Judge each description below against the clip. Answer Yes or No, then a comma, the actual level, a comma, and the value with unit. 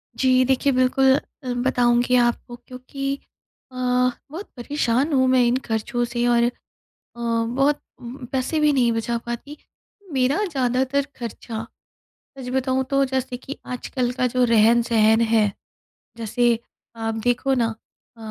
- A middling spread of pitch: No, narrow, 2.0 semitones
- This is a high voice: Yes, very high, 250 Hz